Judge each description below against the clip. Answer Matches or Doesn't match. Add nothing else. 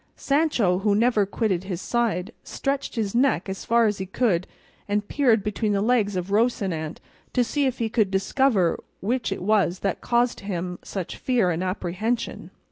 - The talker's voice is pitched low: Doesn't match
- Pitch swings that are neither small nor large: Matches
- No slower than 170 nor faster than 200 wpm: Matches